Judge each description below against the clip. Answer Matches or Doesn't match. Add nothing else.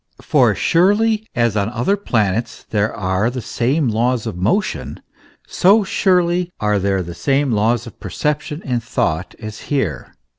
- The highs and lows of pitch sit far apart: Matches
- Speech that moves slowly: Doesn't match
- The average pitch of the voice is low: Matches